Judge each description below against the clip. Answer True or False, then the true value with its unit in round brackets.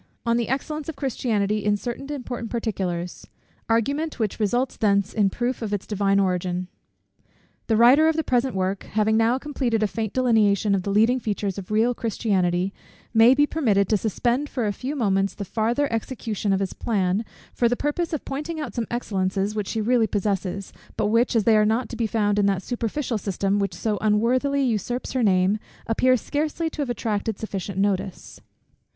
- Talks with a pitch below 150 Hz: False (220 Hz)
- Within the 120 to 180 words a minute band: False (190 wpm)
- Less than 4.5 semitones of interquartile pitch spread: True (3.8 semitones)